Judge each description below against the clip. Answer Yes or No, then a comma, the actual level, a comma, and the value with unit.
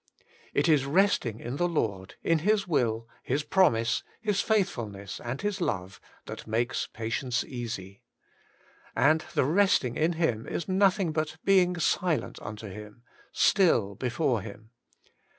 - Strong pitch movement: Yes, wide, 7.8 semitones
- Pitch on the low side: Yes, low, 130 Hz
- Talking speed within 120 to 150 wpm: Yes, average, 140 wpm